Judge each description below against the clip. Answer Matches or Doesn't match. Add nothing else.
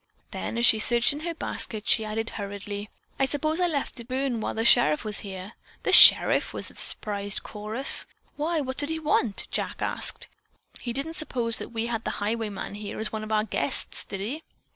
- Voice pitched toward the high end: Matches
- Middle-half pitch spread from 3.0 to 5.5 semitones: Matches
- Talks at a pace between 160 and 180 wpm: Doesn't match